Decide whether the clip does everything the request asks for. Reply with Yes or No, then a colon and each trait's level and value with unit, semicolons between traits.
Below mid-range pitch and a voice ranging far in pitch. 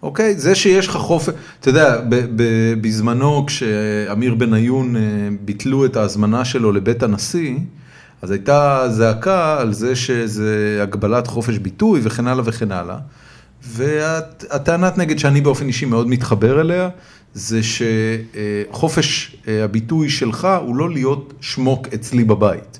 No: low, 125 Hz; average, 4.7 semitones